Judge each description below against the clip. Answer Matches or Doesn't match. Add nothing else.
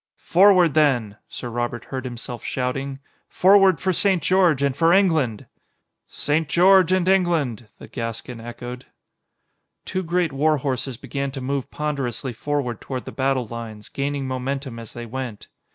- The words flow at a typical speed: Matches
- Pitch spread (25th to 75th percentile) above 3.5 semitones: Matches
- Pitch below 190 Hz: Matches